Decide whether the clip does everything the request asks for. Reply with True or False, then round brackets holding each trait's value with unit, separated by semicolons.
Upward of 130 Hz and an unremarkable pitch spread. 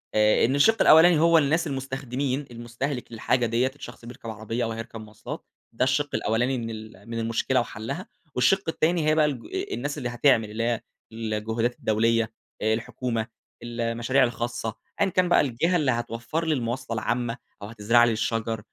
False (120 Hz; 3.4 semitones)